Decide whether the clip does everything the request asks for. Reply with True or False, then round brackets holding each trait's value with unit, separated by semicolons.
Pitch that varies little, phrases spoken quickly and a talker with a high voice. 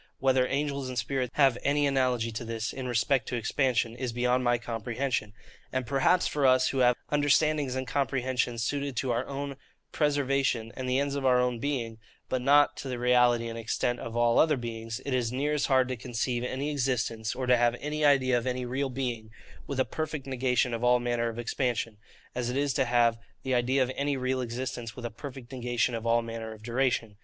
False (2.3 semitones; 210 wpm; 125 Hz)